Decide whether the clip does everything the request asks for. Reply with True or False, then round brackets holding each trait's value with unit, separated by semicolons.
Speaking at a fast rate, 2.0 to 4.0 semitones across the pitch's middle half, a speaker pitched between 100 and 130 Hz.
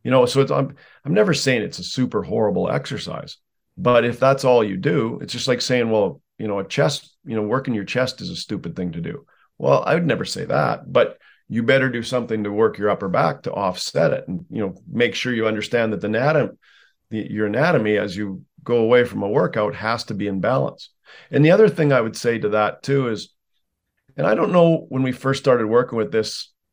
True (235 wpm; 3.5 semitones; 120 Hz)